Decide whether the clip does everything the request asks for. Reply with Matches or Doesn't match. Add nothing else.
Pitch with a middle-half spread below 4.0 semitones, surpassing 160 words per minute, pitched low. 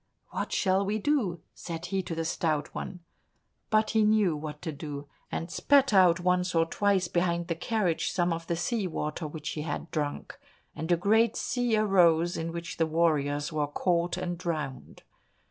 Doesn't match